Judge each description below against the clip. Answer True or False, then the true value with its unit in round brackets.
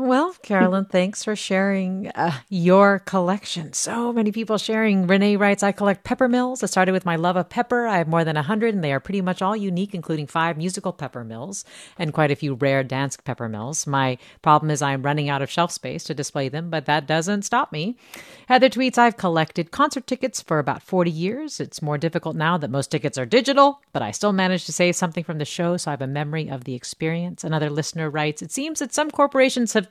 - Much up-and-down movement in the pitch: True (5.9 semitones)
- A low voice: False (180 Hz)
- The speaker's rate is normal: False (225 wpm)